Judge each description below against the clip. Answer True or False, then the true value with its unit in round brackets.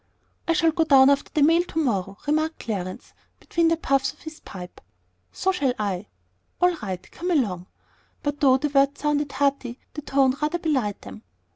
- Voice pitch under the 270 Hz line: False (280 Hz)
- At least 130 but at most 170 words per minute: False (180 wpm)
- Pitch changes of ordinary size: True (4.7 semitones)